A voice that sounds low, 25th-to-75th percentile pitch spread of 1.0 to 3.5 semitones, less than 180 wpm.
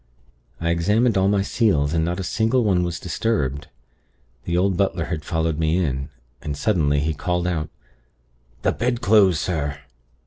No: very low, 85 Hz; average, 4.2 semitones; average, 160 wpm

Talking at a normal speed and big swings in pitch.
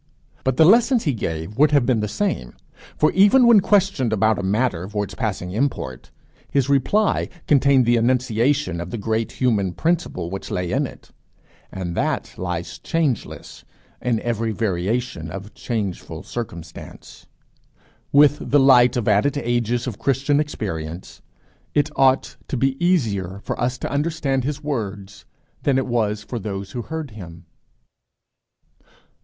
Yes: average, 150 wpm; wide, 6.2 semitones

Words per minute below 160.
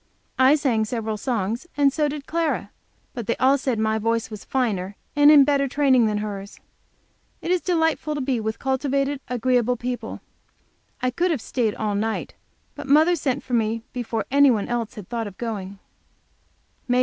No: average, 175 wpm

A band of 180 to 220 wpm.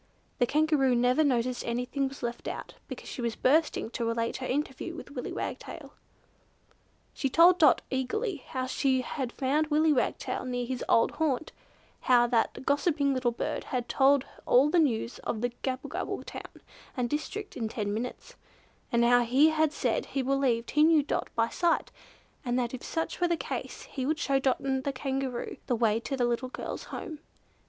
Yes: average, 185 wpm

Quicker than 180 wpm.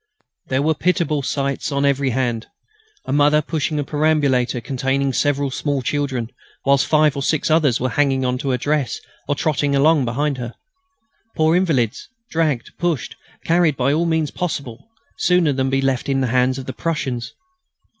No: average, 170 wpm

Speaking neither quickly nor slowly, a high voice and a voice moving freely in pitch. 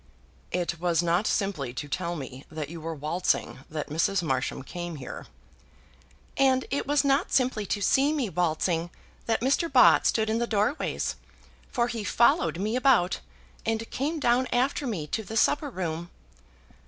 Yes: average, 165 wpm; high, 200 Hz; wide, 7.3 semitones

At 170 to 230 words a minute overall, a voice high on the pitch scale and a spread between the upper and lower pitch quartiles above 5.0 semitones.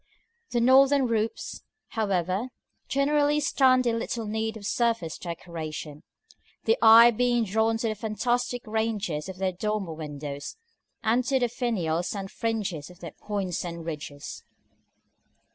No: slow, 135 wpm; high, 220 Hz; wide, 5.4 semitones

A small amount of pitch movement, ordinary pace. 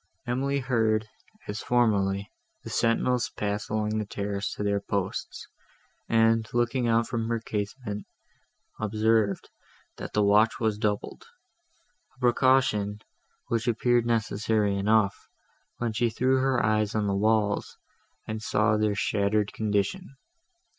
No: narrow, 2.3 semitones; slow, 125 wpm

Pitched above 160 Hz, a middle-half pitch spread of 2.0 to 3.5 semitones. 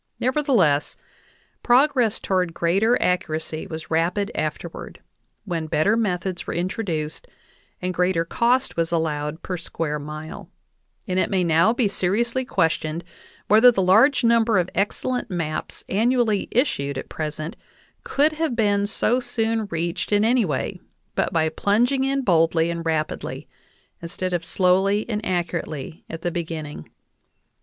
No: medium, 185 Hz; wide, 5.6 semitones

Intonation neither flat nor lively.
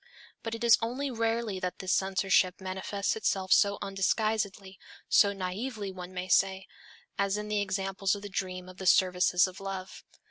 No: narrow, 2.1 semitones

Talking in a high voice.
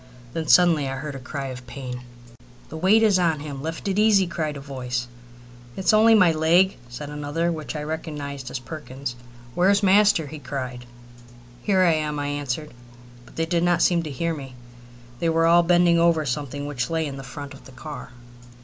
No: medium, 155 Hz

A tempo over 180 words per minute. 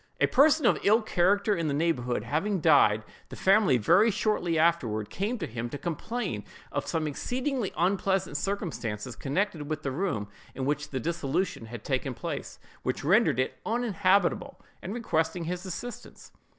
No: average, 160 wpm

